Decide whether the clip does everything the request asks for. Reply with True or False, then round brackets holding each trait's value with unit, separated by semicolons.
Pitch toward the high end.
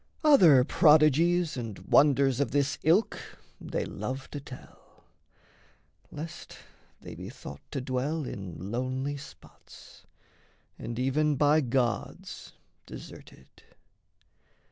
False (140 Hz)